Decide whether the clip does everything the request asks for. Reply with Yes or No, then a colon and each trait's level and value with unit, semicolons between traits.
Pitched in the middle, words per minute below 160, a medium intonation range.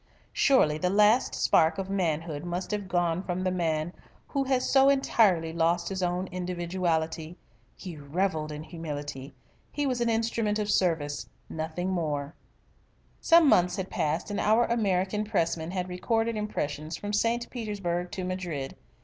Yes: medium, 180 Hz; average, 150 wpm; average, 4.4 semitones